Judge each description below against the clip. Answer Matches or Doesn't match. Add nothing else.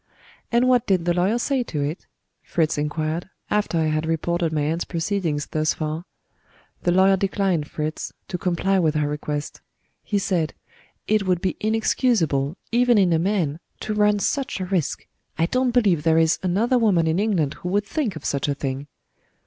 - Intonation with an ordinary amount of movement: Matches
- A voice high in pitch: Doesn't match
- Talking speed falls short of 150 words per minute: Doesn't match